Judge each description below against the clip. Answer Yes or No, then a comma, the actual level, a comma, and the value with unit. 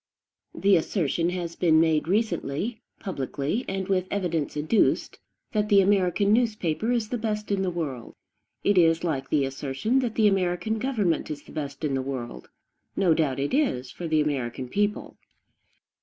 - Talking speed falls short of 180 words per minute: Yes, average, 165 wpm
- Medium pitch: Yes, medium, 175 Hz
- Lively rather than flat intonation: Yes, wide, 5.8 semitones